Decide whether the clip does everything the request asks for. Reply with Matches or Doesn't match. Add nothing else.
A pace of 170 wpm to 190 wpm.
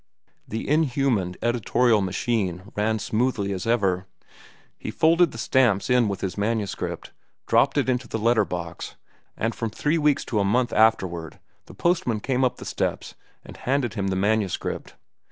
Doesn't match